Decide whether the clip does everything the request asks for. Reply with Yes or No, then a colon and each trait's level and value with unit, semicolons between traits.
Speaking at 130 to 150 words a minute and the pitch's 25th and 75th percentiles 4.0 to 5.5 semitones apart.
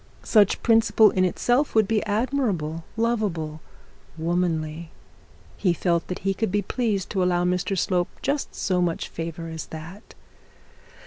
Yes: average, 140 wpm; average, 4.5 semitones